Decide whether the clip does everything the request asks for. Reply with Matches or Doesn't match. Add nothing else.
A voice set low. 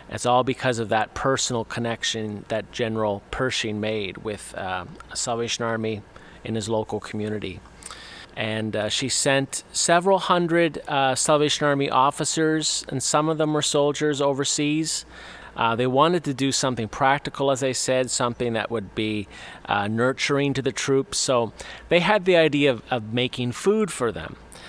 Matches